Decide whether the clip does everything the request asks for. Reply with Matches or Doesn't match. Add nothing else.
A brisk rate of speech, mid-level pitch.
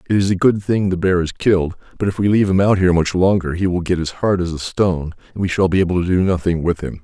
Doesn't match